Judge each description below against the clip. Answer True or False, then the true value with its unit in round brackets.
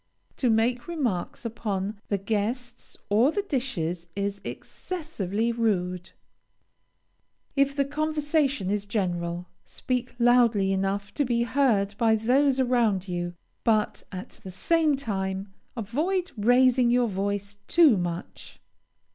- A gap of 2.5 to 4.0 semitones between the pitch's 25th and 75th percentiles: False (4.9 semitones)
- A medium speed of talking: False (120 wpm)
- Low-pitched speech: False (225 Hz)